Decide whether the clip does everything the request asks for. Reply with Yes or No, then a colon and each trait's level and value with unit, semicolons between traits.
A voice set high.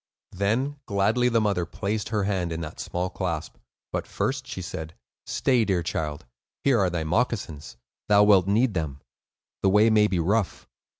No: low, 100 Hz